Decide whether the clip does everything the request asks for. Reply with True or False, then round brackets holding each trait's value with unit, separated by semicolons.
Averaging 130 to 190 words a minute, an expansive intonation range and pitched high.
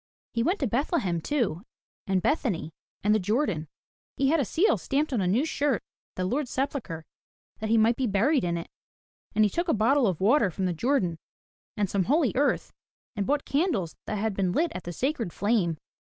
False (205 wpm; 7.1 semitones; 220 Hz)